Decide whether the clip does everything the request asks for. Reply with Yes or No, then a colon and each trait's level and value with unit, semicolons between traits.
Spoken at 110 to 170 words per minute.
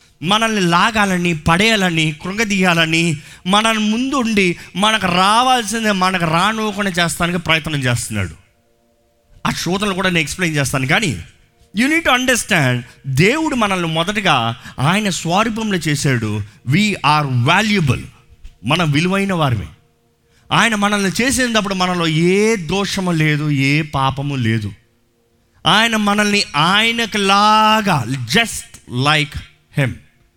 No: average, 100 wpm